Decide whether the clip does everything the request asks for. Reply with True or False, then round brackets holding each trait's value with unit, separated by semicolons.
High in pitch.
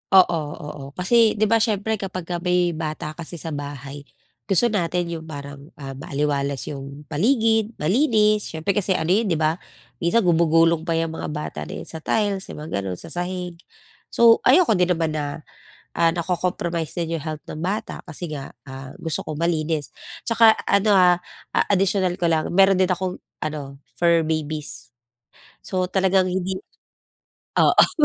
False (170 Hz)